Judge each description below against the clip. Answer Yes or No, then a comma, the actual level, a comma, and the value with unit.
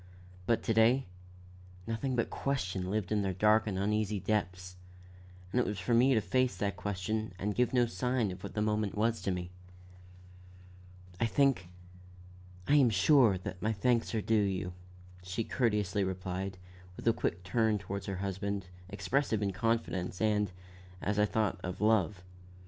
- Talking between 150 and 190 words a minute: Yes, average, 165 wpm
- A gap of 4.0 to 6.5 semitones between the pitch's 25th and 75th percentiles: No, average, 3.2 semitones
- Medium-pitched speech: No, low, 105 Hz